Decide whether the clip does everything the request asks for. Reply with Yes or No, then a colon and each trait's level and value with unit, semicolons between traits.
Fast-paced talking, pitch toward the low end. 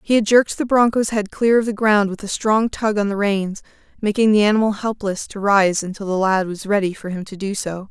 No: fast, 250 wpm; high, 205 Hz